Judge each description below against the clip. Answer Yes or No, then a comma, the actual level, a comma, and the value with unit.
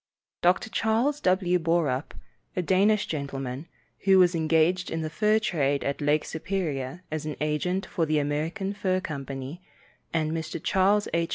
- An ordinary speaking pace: Yes, average, 155 wpm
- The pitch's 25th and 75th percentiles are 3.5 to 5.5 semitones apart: Yes, average, 3.8 semitones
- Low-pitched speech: No, medium, 165 Hz